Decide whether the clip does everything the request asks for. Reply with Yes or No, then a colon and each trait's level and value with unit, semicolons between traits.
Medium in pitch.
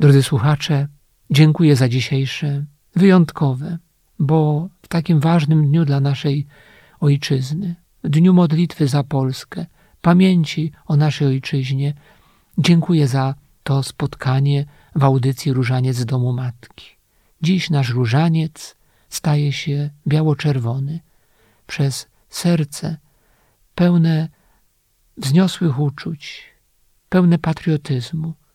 Yes: medium, 145 Hz